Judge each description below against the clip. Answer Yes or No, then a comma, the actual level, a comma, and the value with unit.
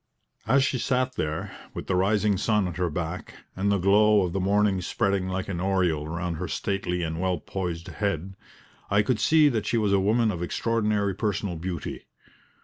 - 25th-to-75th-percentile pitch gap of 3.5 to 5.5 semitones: No, average, 2.9 semitones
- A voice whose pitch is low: Yes, very low, 95 Hz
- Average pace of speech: Yes, average, 190 wpm